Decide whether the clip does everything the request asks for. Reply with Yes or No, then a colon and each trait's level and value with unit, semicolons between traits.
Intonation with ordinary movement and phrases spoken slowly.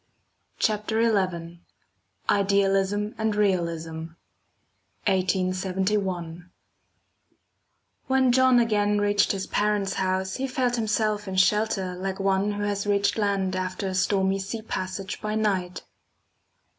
No: narrow, 2.1 semitones; slow, 110 wpm